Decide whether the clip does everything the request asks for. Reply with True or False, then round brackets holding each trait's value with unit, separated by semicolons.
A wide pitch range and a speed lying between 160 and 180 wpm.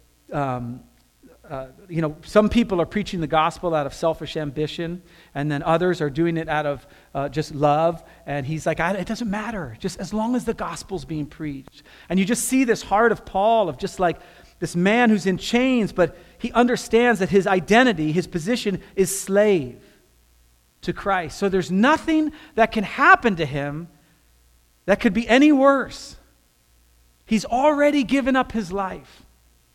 True (6.7 semitones; 175 wpm)